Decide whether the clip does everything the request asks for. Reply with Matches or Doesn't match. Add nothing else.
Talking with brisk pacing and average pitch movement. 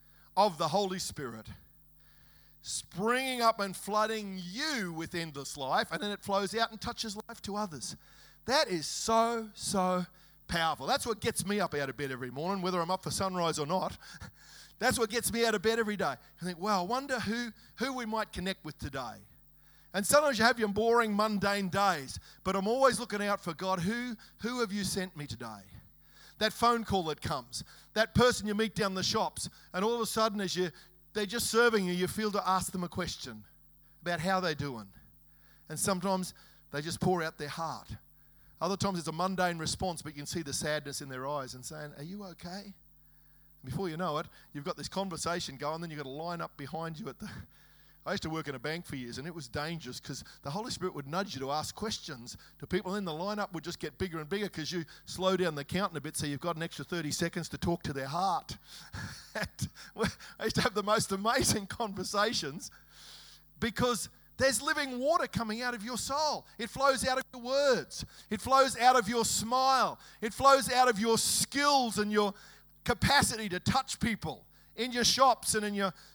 Doesn't match